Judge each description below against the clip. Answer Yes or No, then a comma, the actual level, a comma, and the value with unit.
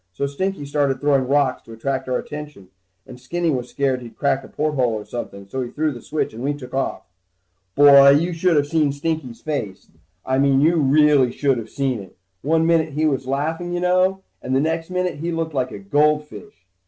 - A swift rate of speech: Yes, fast, 215 wpm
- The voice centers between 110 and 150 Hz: Yes, medium, 140 Hz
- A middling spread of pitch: Yes, average, 3.5 semitones